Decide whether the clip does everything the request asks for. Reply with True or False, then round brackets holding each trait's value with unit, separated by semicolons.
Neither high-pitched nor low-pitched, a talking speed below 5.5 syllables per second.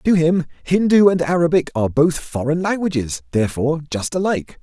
False (160 Hz; 5.8 syllables/s)